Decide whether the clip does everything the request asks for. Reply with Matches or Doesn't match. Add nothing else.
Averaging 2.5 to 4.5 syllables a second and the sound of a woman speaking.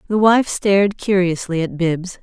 Matches